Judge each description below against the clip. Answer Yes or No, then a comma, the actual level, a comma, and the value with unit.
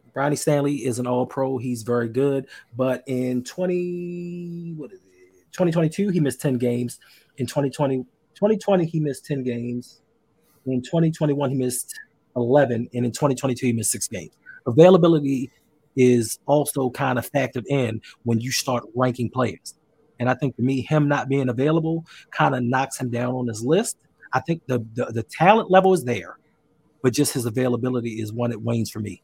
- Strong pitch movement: No, average, 3.6 semitones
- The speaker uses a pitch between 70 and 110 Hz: No, low, 130 Hz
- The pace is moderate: Yes, average, 180 wpm